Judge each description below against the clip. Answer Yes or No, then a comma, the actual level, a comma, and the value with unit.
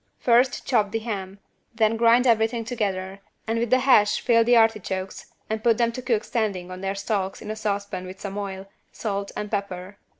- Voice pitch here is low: No, high, 215 Hz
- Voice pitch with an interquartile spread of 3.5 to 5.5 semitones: No, average, 2.9 semitones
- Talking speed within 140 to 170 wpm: No, average, 195 wpm